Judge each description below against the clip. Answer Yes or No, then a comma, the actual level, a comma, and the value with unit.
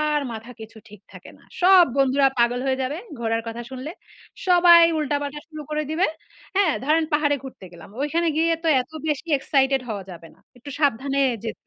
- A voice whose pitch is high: Yes, very high, 280 Hz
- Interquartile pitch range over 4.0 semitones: Yes, average, 4.6 semitones